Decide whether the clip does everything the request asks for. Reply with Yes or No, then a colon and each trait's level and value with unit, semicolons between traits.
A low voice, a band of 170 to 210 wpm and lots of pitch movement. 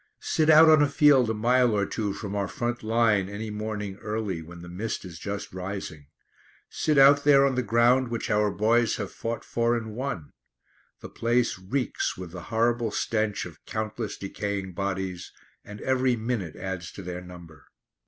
No: low, 110 Hz; average, 180 wpm; average, 3.9 semitones